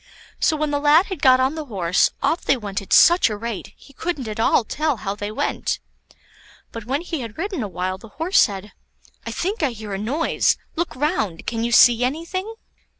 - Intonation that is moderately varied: No, wide, 6.9 semitones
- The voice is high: Yes, very high, 255 Hz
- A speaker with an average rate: No, fast, 210 wpm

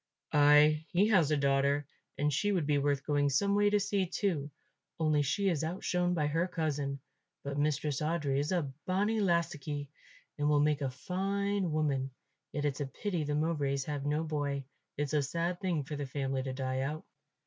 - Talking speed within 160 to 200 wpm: Yes, average, 190 wpm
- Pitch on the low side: No, medium, 150 Hz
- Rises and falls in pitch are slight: No, average, 3.5 semitones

